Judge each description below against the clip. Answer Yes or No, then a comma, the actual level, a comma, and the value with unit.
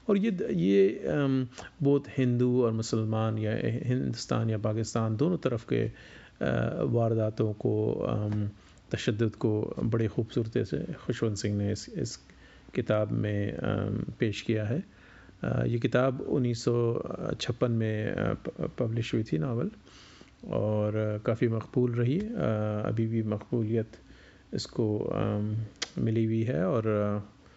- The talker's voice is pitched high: No, low, 115 Hz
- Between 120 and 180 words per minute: No, slow, 110 wpm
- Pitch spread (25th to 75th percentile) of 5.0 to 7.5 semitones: No, narrow, 2.6 semitones